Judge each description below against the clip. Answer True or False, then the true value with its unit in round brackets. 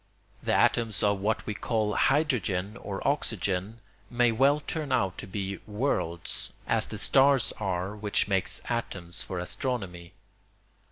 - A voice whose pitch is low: True (105 Hz)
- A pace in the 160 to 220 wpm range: False (135 wpm)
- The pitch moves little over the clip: False (4.4 semitones)